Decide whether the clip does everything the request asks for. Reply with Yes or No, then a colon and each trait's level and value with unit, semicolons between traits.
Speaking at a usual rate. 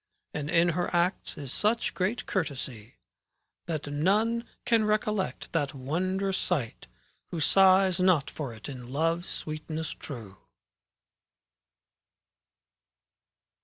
No: slow, 105 wpm